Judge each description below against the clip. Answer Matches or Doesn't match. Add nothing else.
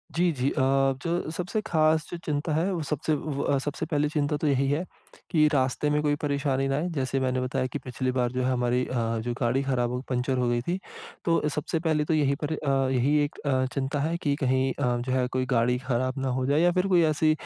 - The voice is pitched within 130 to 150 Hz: Matches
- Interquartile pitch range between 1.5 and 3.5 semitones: Matches